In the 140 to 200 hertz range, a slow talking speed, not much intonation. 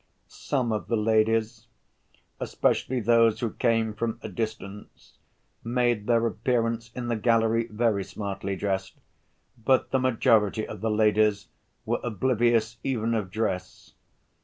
No: low, 115 Hz; slow, 130 wpm; narrow, 1.7 semitones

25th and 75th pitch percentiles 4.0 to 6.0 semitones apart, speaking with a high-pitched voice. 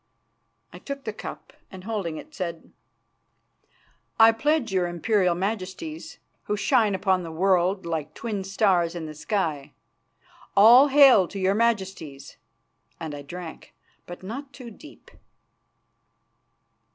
Yes: average, 4.6 semitones; high, 195 Hz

